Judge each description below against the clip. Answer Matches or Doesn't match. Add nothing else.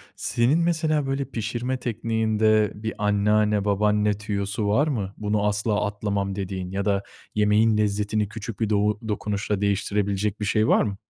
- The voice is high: Doesn't match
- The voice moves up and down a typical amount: Doesn't match